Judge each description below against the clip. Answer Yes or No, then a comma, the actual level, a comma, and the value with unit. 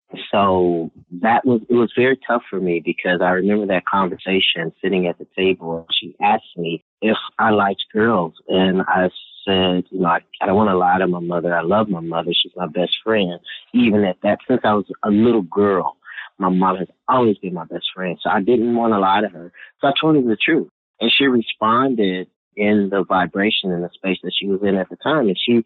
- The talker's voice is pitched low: Yes, very low, 95 Hz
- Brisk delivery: Yes, fast, 225 wpm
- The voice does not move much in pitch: No, average, 3.2 semitones